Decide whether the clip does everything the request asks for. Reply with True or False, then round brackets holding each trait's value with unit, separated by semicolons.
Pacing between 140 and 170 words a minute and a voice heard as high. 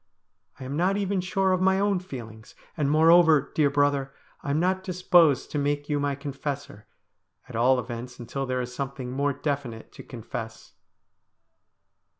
False (160 wpm; 140 Hz)